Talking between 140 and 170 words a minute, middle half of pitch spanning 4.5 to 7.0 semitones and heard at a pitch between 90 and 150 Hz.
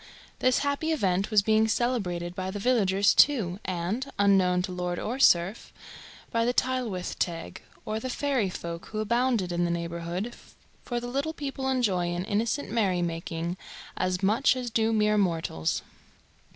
No: average, 160 wpm; average, 5.3 semitones; high, 205 Hz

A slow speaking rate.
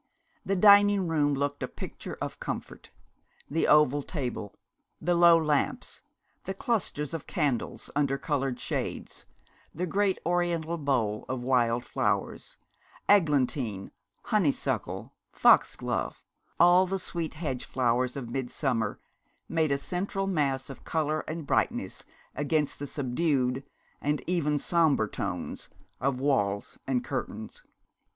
Yes: slow, 120 wpm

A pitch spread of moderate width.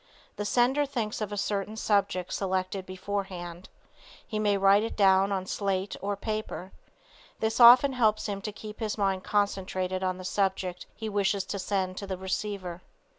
No: narrow, 2.2 semitones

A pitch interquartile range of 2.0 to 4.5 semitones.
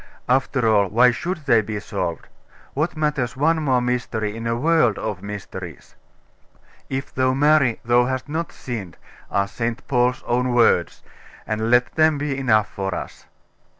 Yes: average, 3.9 semitones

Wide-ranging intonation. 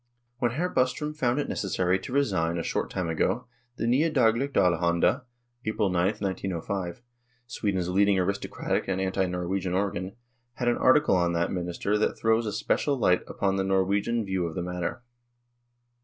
No: average, 4.8 semitones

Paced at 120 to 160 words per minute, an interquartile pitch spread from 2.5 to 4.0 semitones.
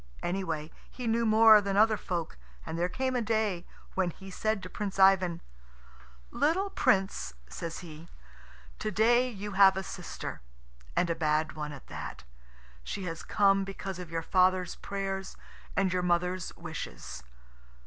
Yes: average, 155 wpm; average, 3.6 semitones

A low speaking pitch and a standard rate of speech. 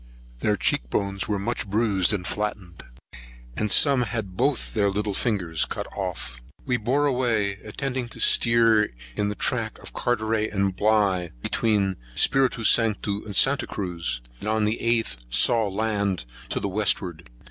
Yes: low, 105 Hz; average, 160 wpm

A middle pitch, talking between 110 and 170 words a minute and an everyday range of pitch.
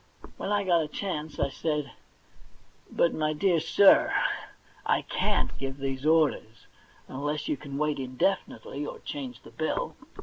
Yes: medium, 150 Hz; average, 145 wpm; average, 3.6 semitones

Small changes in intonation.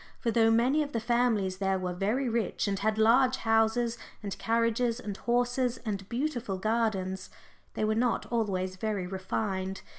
No: average, 3.5 semitones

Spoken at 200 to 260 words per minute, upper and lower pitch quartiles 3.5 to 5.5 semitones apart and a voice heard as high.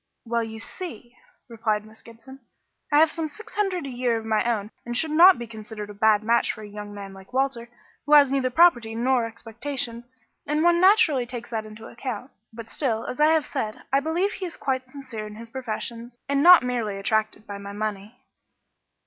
Yes: fast, 205 wpm; average, 4.3 semitones; high, 235 Hz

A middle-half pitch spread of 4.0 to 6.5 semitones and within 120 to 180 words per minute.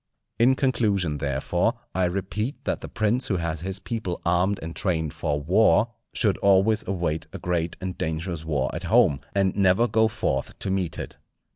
Yes: average, 4.4 semitones; average, 175 wpm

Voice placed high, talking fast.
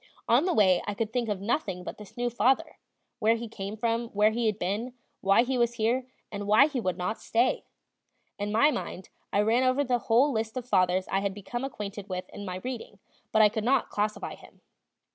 Yes: high, 220 Hz; fast, 220 wpm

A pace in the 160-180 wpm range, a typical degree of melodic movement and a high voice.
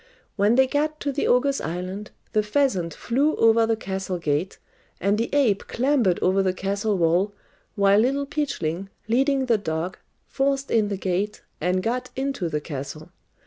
No: average, 165 wpm; wide, 6.3 semitones; high, 210 Hz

